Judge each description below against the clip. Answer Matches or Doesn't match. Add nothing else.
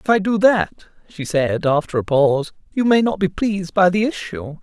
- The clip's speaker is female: Doesn't match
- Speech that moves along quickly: Matches